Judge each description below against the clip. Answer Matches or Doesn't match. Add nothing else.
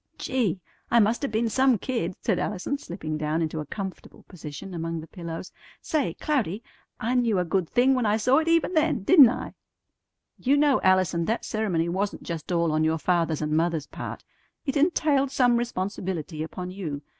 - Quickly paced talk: Doesn't match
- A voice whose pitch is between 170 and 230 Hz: Matches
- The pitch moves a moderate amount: Doesn't match